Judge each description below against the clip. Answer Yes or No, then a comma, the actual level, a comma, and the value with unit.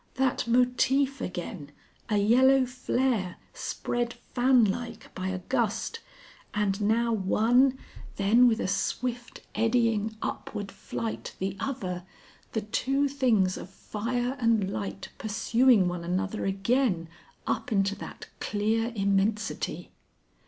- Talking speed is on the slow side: Yes, slow, 115 wpm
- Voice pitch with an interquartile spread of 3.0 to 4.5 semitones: Yes, average, 4.1 semitones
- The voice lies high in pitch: Yes, high, 225 Hz